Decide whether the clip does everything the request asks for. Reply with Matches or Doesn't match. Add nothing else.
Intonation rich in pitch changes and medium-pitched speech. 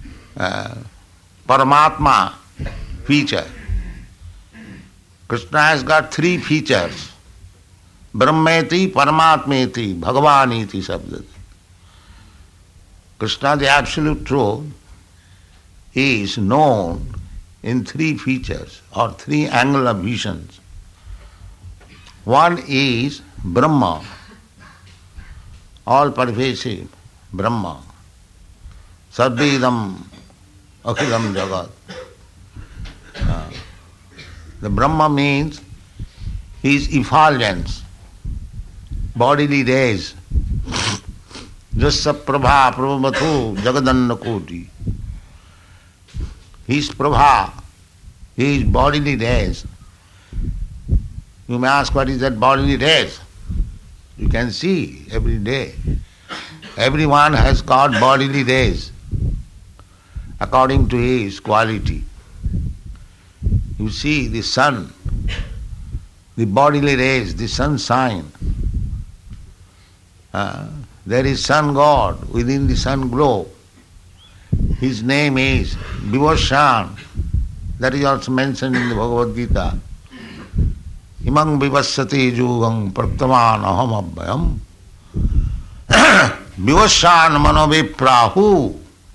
Doesn't match